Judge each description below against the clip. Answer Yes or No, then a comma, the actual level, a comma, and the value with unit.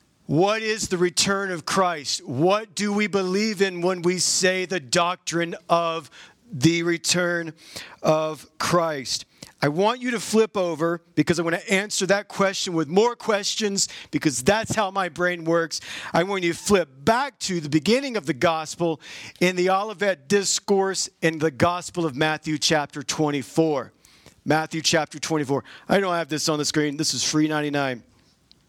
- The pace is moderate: Yes, average, 165 wpm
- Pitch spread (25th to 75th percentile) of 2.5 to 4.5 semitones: Yes, average, 3.8 semitones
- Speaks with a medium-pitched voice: Yes, medium, 170 Hz